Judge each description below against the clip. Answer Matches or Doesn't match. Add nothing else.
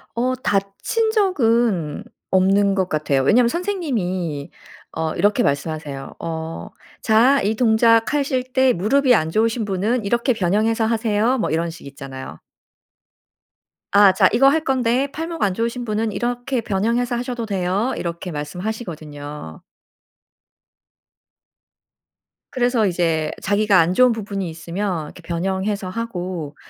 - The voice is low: Doesn't match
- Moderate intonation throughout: Doesn't match